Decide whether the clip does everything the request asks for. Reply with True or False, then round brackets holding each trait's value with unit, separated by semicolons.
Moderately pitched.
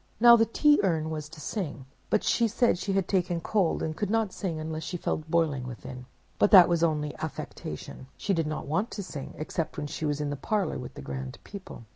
True (160 Hz)